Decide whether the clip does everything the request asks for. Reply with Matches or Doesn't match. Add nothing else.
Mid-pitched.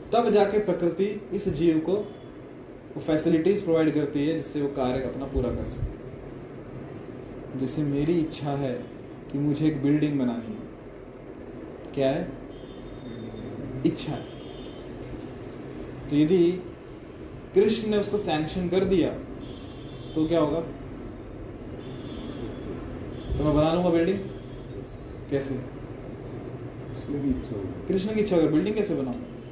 Matches